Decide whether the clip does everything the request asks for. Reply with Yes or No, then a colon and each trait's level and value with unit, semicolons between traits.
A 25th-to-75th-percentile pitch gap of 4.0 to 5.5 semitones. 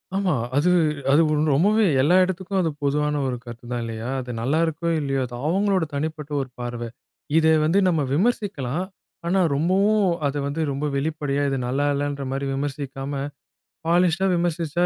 Yes: average, 4.3 semitones